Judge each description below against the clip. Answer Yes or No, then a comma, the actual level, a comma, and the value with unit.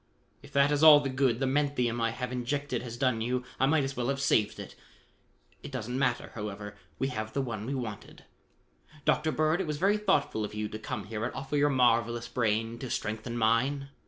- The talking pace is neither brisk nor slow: No, fast, 215 wpm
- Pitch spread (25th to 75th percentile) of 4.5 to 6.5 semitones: No, average, 3.6 semitones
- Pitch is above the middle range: No, low, 125 Hz